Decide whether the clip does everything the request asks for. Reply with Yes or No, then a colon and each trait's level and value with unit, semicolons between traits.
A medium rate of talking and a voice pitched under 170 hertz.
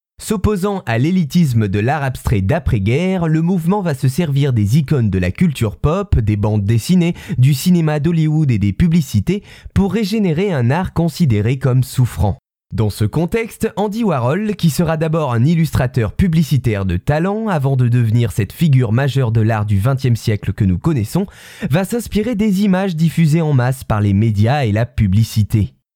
Yes: average, 170 wpm; medium, 140 Hz